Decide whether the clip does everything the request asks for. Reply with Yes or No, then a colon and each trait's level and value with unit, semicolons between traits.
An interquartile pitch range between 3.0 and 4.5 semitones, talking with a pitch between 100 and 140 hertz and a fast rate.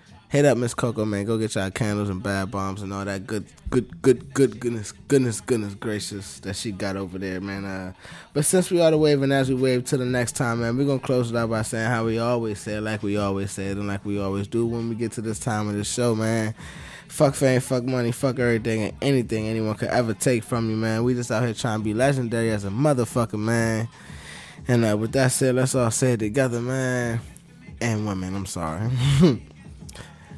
Yes: average, 3.4 semitones; low, 115 Hz; fast, 240 wpm